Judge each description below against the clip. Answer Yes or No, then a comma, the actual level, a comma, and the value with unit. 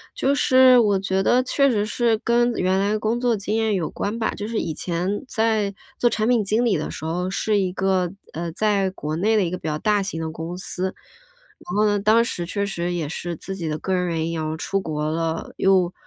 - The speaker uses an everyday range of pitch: Yes, average, 4.0 semitones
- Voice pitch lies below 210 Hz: Yes, high, 195 Hz